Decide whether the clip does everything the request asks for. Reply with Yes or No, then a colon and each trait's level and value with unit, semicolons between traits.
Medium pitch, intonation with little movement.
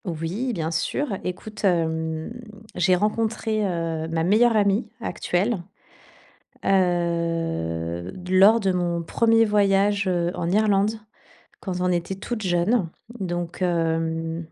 No: medium, 180 Hz; average, 3.7 semitones